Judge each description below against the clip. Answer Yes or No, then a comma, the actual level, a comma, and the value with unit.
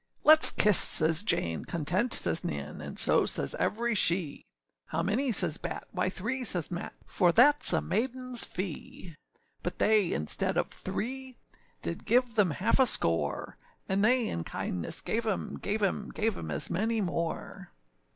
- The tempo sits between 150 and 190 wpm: Yes, average, 165 wpm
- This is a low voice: No, high, 205 Hz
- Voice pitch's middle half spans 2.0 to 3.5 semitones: No, wide, 5.6 semitones